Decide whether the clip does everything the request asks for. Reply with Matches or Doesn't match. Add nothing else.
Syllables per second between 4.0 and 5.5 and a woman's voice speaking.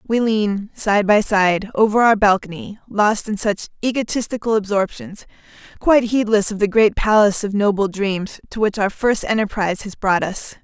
Matches